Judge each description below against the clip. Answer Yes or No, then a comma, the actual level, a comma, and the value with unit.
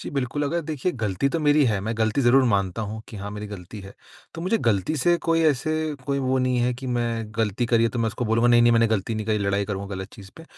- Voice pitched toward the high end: No, low, 115 Hz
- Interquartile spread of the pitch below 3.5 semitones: No, average, 4.4 semitones